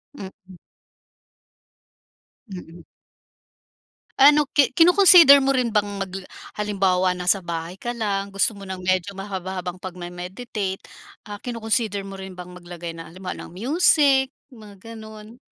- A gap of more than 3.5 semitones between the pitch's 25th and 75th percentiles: Yes, average, 4.5 semitones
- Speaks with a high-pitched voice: Yes, high, 195 Hz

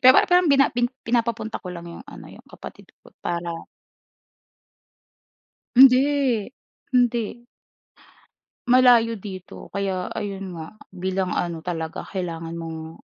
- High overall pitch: Yes, high, 200 Hz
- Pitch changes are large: Yes, wide, 5.9 semitones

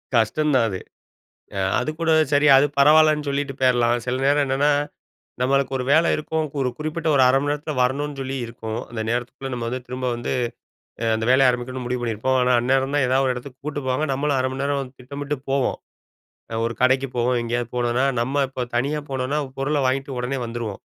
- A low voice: Yes, low, 130 Hz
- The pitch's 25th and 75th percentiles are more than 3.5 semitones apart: No, narrow, 2.5 semitones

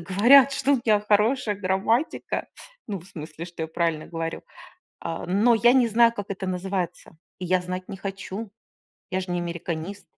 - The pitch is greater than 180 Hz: Yes, high, 190 Hz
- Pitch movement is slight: No, average, 4.0 semitones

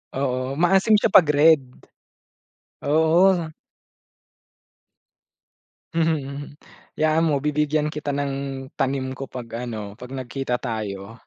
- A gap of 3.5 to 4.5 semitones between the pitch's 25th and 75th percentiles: Yes, average, 3.8 semitones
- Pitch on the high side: No, medium, 140 Hz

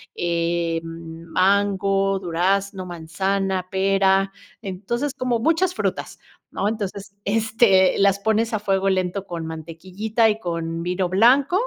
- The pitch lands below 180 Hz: No, high, 195 Hz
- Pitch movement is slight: No, average, 3.0 semitones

